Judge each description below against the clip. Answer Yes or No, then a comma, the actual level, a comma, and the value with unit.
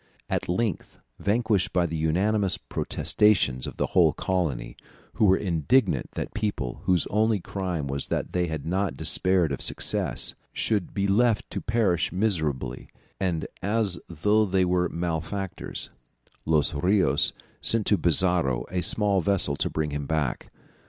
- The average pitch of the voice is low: Yes, very low, 90 Hz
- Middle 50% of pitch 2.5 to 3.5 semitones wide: No, average, 4.3 semitones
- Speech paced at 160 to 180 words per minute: No, average, 145 wpm